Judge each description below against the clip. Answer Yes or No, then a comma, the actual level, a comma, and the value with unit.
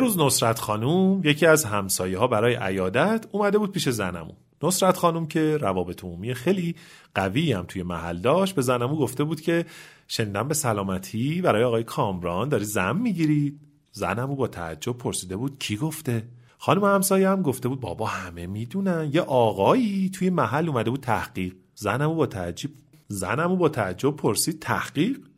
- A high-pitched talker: No, low, 135 Hz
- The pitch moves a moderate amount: No, wide, 7.6 semitones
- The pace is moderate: No, fast, 160 wpm